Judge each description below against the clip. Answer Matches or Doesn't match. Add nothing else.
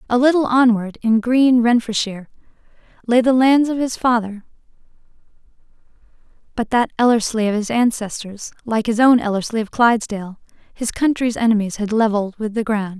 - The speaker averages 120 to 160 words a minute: Matches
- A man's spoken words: Doesn't match